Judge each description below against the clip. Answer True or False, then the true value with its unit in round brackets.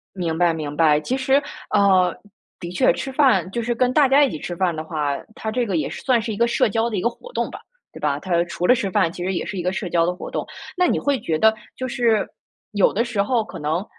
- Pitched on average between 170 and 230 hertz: True (200 Hz)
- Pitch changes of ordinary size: False (5.7 semitones)